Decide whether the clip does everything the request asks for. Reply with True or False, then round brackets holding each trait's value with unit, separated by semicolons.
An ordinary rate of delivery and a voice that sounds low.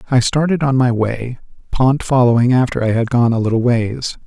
True (195 wpm; 125 Hz)